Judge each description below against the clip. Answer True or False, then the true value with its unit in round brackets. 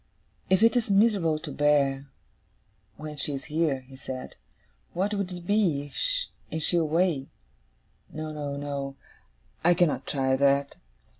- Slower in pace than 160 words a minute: True (140 wpm)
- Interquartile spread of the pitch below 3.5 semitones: False (4.1 semitones)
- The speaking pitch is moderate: True (150 Hz)